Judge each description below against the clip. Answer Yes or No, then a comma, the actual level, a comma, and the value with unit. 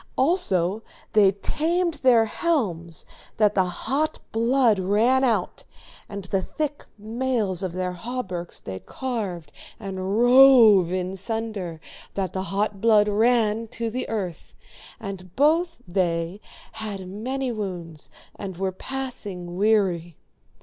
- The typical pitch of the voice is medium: No, high, 210 Hz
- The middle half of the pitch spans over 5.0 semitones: No, average, 4.7 semitones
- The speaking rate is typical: No, slow, 120 wpm